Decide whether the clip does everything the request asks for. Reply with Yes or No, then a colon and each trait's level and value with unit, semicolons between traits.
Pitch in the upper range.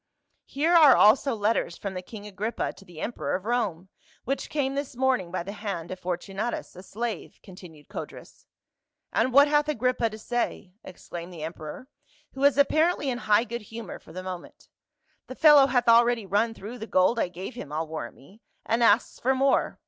Yes: high, 225 Hz